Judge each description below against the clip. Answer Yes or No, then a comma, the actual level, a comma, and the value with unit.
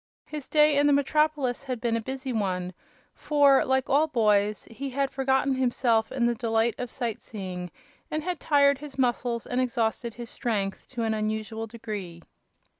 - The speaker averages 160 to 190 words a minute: Yes, average, 175 wpm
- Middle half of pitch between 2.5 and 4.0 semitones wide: Yes, average, 3.7 semitones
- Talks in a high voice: Yes, high, 245 Hz